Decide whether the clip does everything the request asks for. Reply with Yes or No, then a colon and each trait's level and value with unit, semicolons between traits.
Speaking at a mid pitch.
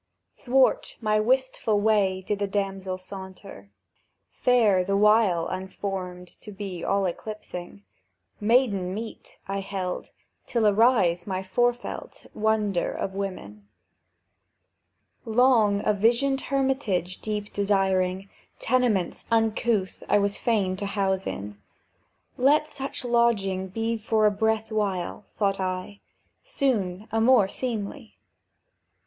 No: high, 205 Hz